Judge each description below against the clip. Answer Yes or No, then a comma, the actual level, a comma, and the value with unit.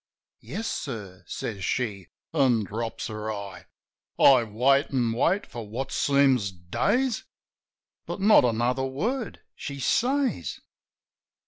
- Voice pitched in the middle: No, low, 125 Hz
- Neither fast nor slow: No, slow, 115 wpm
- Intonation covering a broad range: No, average, 4.9 semitones